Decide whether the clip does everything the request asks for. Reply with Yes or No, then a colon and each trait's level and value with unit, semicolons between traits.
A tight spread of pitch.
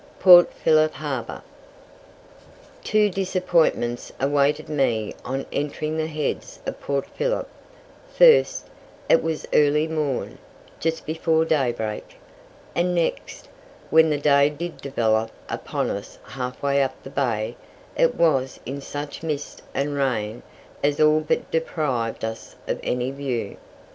No: average, 3.6 semitones